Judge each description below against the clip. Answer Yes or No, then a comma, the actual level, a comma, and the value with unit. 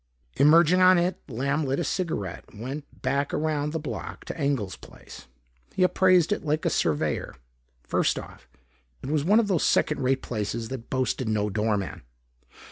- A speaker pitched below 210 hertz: Yes, medium, 140 Hz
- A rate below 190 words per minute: Yes, average, 170 wpm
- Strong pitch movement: Yes, wide, 5.9 semitones